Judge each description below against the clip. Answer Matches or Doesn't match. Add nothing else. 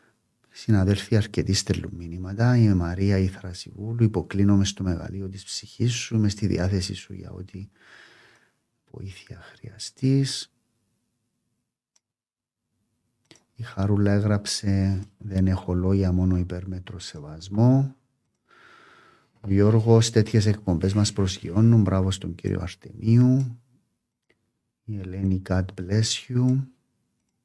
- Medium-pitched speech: Doesn't match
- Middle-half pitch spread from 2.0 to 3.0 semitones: Doesn't match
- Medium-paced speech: Doesn't match